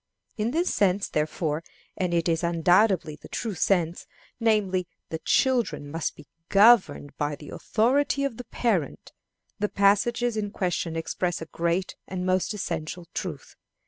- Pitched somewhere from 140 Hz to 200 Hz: Yes, medium, 185 Hz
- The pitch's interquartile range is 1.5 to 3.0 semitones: No, average, 4.7 semitones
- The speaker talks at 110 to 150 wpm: Yes, average, 145 wpm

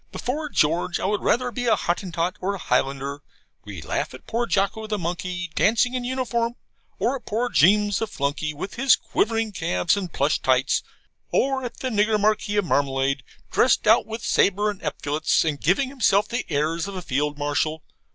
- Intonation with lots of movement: Yes, wide, 6.9 semitones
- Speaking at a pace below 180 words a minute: No, average, 185 wpm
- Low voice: No, high, 200 Hz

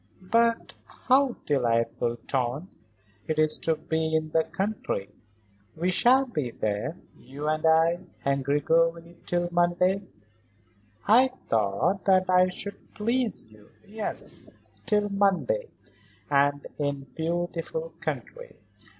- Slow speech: Yes, slow, 115 wpm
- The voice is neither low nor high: Yes, medium, 170 Hz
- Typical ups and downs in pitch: No, wide, 6.0 semitones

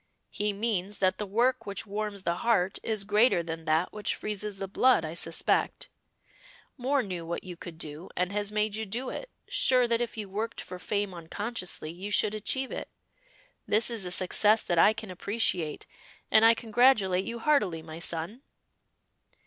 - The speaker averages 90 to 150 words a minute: No, average, 180 wpm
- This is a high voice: Yes, high, 205 Hz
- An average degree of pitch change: Yes, average, 3.9 semitones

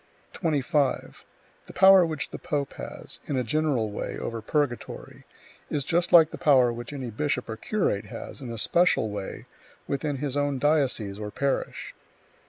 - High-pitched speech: No, medium, 140 Hz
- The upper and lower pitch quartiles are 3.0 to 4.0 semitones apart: No, average, 4.4 semitones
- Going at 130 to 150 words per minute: No, average, 165 wpm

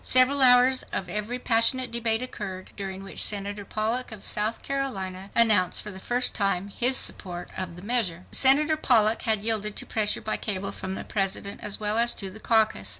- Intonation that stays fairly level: No, average, 3.8 semitones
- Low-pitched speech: No, high, 215 Hz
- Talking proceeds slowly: No, average, 190 wpm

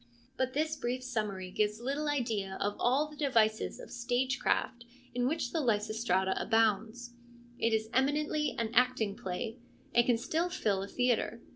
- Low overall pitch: No, high, 240 Hz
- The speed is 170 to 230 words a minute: No, average, 160 wpm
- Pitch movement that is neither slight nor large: Yes, average, 3.3 semitones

